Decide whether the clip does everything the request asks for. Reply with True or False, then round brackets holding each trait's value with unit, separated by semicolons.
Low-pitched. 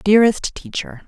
False (190 Hz)